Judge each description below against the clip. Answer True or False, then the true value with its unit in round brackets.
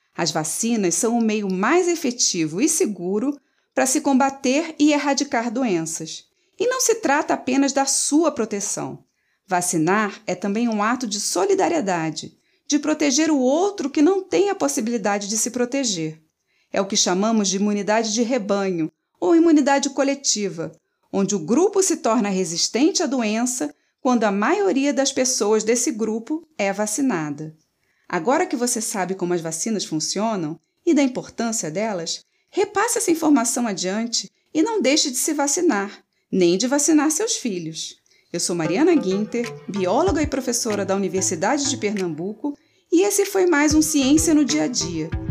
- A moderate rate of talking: True (155 wpm)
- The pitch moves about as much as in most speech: False (7.3 semitones)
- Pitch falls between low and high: False (245 Hz)